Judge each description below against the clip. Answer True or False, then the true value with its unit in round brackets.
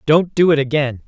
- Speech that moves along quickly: True (225 wpm)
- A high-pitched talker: False (150 Hz)